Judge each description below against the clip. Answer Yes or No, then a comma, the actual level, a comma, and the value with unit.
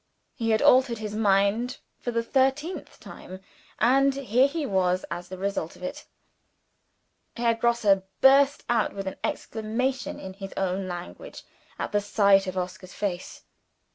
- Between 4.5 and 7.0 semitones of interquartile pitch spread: Yes, average, 5.0 semitones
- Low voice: No, high, 215 Hz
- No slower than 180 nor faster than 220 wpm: No, average, 150 wpm